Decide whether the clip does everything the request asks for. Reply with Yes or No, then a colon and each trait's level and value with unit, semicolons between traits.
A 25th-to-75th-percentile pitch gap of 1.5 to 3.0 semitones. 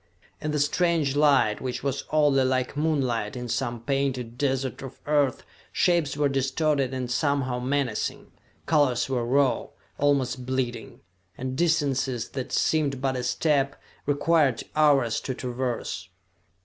Yes: narrow, 2.5 semitones